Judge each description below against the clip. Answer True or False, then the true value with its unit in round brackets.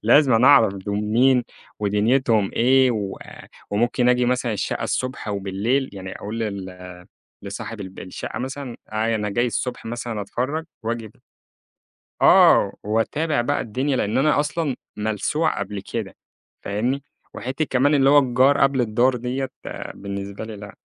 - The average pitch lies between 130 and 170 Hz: False (120 Hz)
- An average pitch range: True (4.2 semitones)